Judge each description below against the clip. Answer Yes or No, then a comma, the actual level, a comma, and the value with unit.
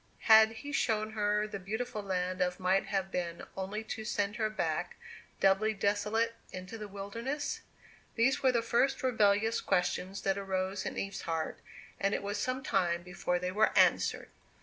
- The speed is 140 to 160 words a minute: No, average, 170 wpm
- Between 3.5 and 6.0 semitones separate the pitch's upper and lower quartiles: No, average, 2.8 semitones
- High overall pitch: Yes, high, 205 Hz